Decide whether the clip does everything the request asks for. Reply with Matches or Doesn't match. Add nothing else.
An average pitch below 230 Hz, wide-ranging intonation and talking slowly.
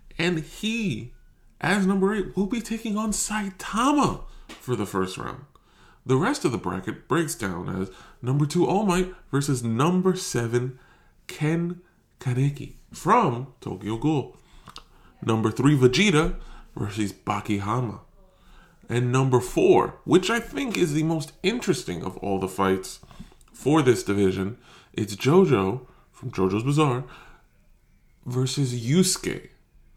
Matches